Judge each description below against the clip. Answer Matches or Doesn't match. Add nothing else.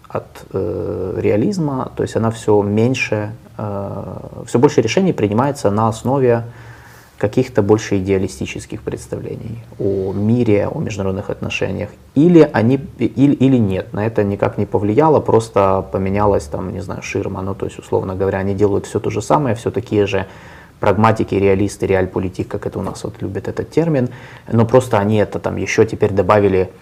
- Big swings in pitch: Doesn't match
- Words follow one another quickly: Matches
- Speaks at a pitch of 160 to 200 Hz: Doesn't match